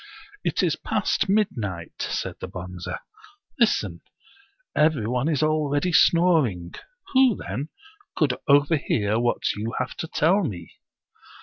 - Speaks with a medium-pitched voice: Yes, medium, 145 Hz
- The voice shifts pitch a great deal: Yes, wide, 7.6 semitones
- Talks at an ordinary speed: No, slow, 130 wpm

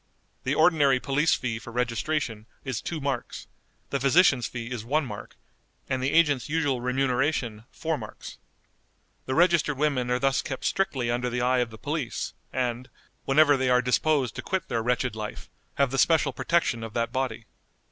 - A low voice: Yes, low, 130 Hz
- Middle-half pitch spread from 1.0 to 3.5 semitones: Yes, average, 3.2 semitones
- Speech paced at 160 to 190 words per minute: Yes, average, 175 wpm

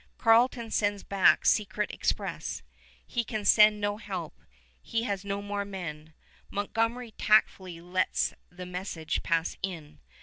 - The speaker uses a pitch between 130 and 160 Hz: No, high, 200 Hz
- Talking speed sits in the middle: No, slow, 130 wpm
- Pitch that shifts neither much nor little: Yes, average, 3.0 semitones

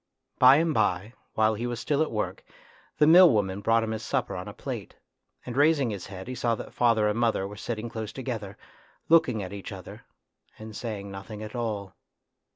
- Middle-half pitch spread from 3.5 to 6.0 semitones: No, average, 3.1 semitones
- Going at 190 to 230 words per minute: Yes, average, 200 wpm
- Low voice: Yes, low, 110 Hz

